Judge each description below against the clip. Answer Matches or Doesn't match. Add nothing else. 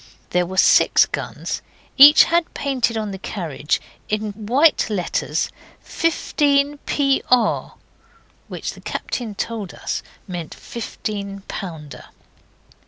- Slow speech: Matches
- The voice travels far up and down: Matches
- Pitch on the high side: Matches